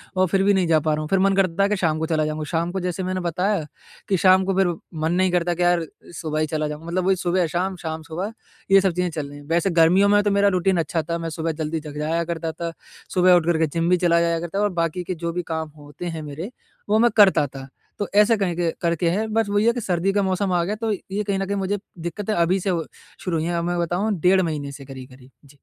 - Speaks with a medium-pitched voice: Yes, medium, 175 Hz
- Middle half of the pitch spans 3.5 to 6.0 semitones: No, average, 3.1 semitones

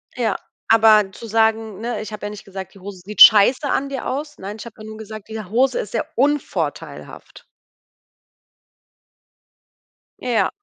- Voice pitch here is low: No, high, 220 Hz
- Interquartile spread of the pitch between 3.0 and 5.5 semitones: No, narrow, 2.6 semitones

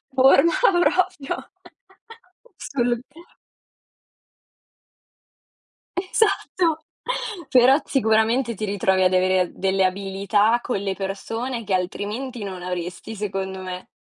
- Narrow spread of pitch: No, average, 5.3 semitones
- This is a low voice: No, high, 210 Hz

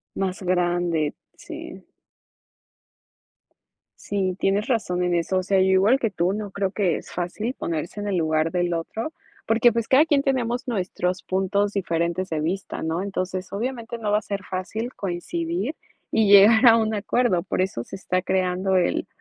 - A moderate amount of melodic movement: Yes, average, 3.5 semitones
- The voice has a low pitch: No, high, 190 Hz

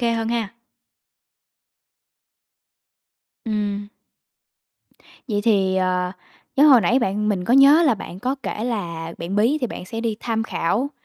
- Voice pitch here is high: Yes, high, 215 Hz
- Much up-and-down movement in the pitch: No, average, 3.8 semitones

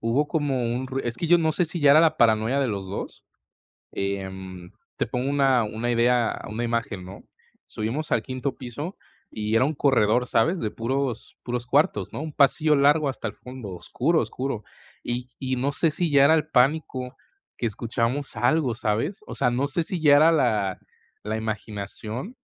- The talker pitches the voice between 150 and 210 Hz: No, low, 125 Hz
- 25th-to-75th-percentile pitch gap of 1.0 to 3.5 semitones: No, average, 4.5 semitones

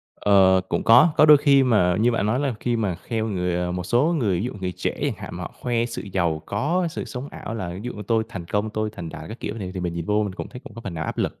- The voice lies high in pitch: No, low, 105 Hz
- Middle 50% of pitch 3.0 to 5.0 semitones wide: Yes, average, 4.7 semitones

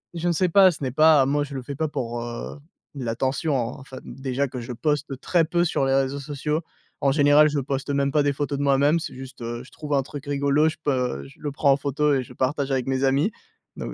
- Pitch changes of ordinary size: No, narrow, 2.1 semitones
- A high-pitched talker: No, medium, 140 Hz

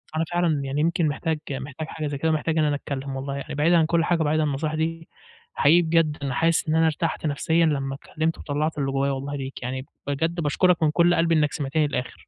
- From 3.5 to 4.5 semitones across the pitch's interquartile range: No, narrow, 2.6 semitones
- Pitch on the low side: No, medium, 155 Hz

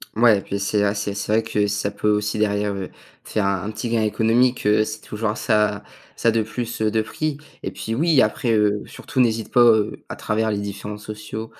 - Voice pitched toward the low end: Yes, low, 105 Hz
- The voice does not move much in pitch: Yes, narrow, 1.5 semitones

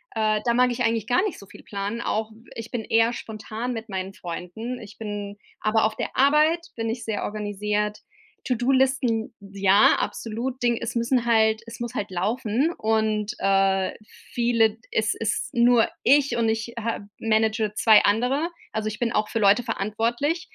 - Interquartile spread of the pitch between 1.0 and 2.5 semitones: Yes, narrow, 2.1 semitones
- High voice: Yes, high, 225 Hz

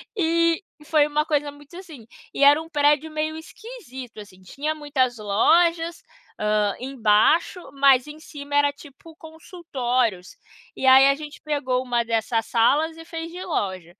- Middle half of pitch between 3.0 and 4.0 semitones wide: No, average, 4.5 semitones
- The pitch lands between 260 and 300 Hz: Yes, very high, 290 Hz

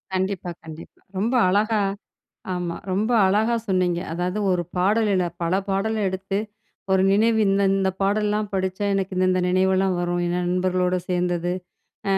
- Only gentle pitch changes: Yes, narrow, 2.1 semitones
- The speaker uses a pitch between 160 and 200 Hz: Yes, high, 190 Hz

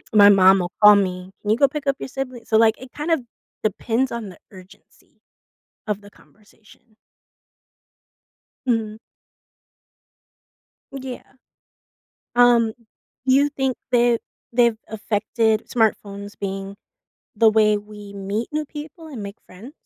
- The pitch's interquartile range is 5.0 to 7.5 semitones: No, average, 3.7 semitones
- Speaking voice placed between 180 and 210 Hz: No, high, 220 Hz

